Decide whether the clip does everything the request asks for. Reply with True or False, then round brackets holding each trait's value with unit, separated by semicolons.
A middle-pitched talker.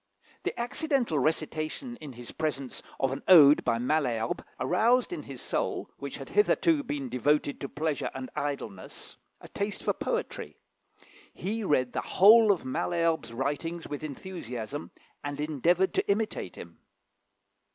True (155 Hz)